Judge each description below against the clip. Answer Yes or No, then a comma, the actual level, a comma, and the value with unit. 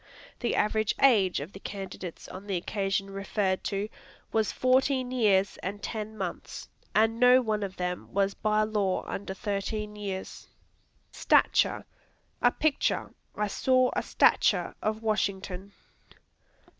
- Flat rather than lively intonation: Yes, narrow, 2.2 semitones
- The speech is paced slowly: Yes, slow, 130 wpm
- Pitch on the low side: No, high, 205 Hz